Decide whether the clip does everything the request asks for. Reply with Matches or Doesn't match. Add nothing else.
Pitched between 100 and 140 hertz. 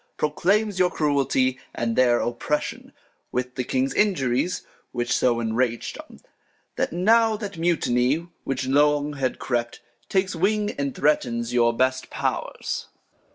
Matches